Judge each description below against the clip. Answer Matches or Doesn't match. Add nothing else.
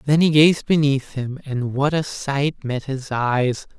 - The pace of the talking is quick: Doesn't match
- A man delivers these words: Matches